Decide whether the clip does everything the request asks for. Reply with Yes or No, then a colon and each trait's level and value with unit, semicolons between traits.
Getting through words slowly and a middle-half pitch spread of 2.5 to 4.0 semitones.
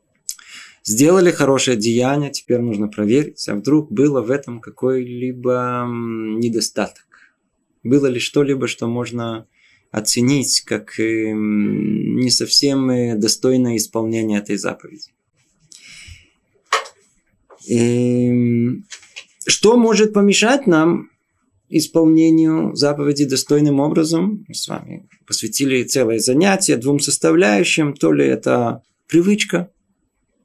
No: slow, 95 wpm; average, 4.9 semitones